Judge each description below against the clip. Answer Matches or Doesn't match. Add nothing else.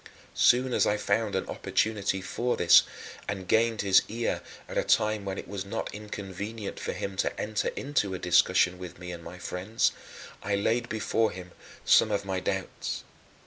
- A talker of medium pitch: Doesn't match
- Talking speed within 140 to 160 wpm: Doesn't match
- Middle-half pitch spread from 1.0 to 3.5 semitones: Matches